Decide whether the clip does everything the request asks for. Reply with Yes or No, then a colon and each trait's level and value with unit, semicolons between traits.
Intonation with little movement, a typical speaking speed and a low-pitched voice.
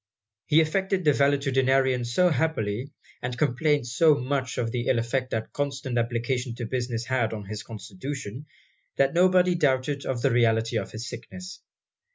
No: average, 3.6 semitones; average, 160 wpm; low, 130 Hz